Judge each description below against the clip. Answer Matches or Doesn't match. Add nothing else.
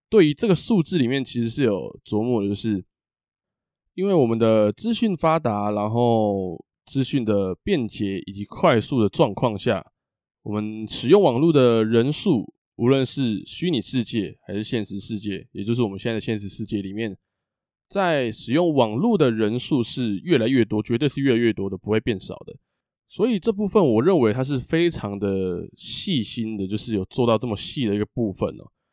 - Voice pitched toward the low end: Matches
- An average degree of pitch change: Matches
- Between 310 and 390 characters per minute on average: Doesn't match